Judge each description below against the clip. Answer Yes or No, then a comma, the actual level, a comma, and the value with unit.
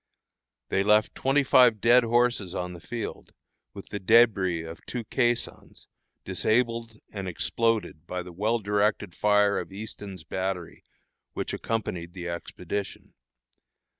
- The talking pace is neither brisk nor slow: No, slow, 130 wpm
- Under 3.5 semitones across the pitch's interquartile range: No, average, 4.1 semitones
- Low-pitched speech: Yes, low, 105 Hz